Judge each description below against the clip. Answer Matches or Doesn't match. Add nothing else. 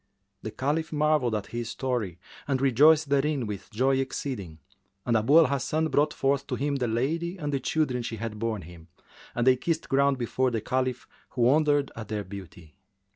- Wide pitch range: Doesn't match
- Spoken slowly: Doesn't match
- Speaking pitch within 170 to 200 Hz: Doesn't match